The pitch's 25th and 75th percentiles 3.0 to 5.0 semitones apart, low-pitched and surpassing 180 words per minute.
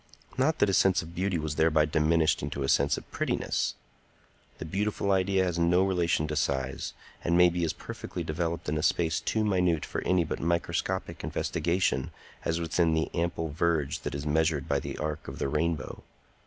No: narrow, 2.5 semitones; very low, 85 Hz; average, 190 wpm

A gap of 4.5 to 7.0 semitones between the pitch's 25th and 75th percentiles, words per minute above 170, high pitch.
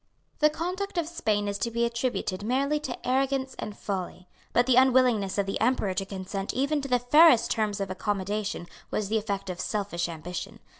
Yes: average, 4.9 semitones; average, 190 wpm; high, 220 Hz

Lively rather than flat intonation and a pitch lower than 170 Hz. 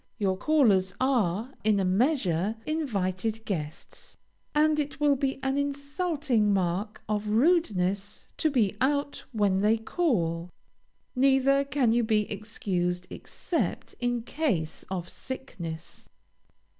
No: wide, 6.4 semitones; high, 225 Hz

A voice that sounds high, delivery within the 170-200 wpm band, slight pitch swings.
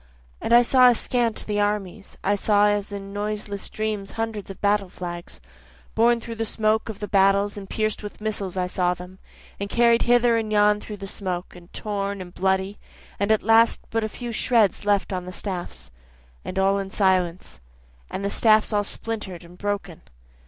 Yes: high, 205 Hz; average, 190 wpm; narrow, 2.2 semitones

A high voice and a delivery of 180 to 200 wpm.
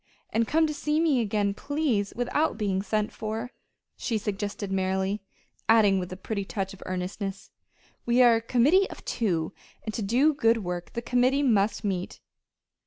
No: high, 215 Hz; average, 170 wpm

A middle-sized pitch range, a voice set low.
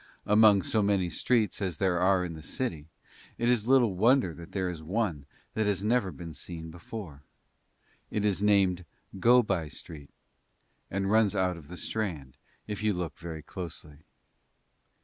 Yes: average, 4.1 semitones; very low, 95 Hz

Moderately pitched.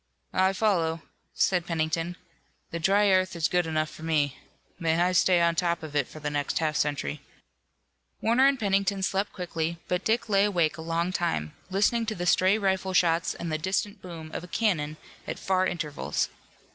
Yes: medium, 175 Hz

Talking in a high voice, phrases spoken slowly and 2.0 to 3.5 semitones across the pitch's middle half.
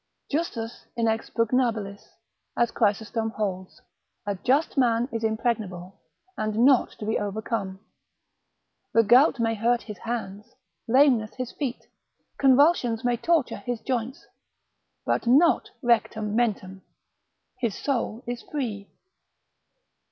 Yes: high, 230 Hz; slow, 110 wpm; average, 2.7 semitones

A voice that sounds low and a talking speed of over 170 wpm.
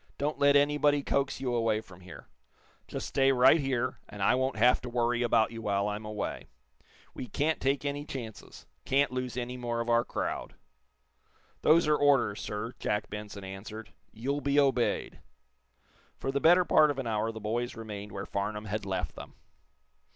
Yes: low, 120 Hz; average, 180 wpm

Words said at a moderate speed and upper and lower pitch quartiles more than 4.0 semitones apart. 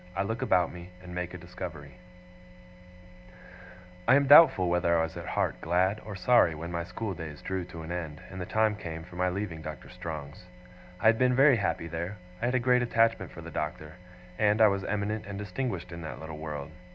No: fast, 215 wpm; average, 4.7 semitones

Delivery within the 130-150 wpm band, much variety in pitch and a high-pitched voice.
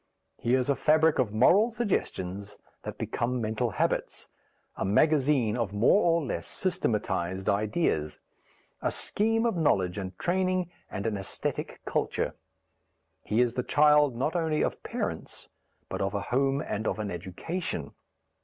No: average, 145 wpm; wide, 7.8 semitones; low, 125 Hz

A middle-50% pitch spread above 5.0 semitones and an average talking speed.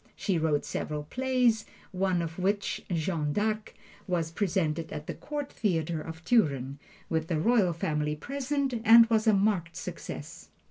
Yes: wide, 5.5 semitones; average, 150 wpm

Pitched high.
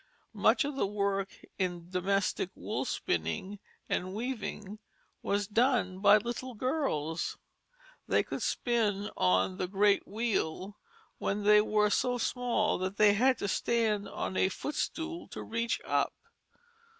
Yes: high, 205 Hz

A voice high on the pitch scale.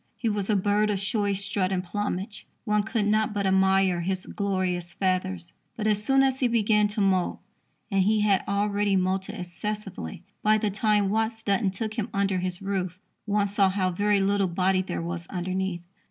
Yes: high, 200 Hz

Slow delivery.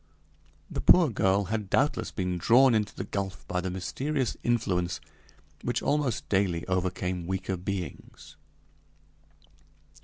Yes: slow, 120 wpm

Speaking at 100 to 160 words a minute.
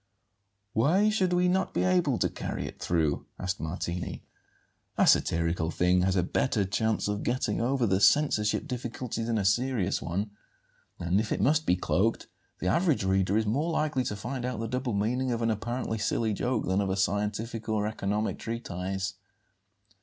No: average, 175 wpm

